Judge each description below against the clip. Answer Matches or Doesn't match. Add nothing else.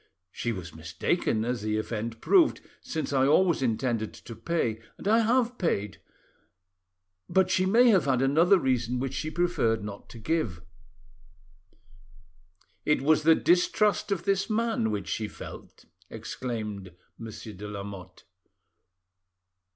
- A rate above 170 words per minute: Doesn't match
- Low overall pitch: Matches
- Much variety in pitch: Matches